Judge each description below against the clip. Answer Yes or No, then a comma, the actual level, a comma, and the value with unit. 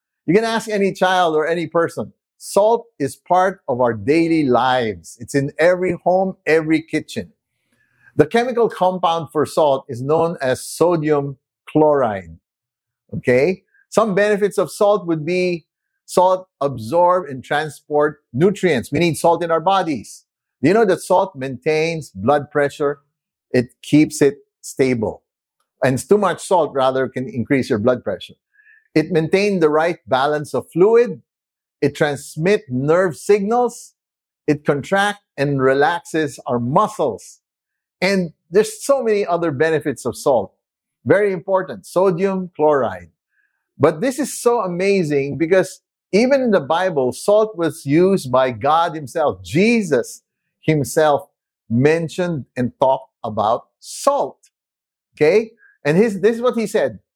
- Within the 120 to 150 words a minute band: Yes, average, 140 wpm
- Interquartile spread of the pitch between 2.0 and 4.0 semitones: No, wide, 5.5 semitones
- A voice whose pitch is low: No, medium, 165 Hz